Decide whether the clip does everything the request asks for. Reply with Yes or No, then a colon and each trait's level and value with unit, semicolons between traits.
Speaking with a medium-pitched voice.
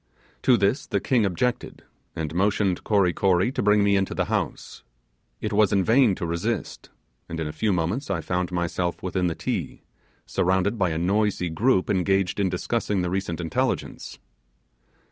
No: very low, 95 Hz